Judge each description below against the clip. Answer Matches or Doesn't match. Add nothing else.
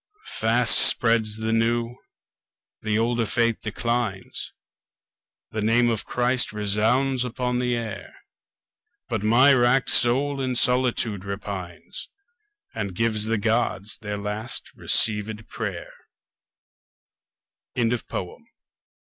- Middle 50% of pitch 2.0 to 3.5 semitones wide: Matches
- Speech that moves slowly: Matches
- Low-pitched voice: Matches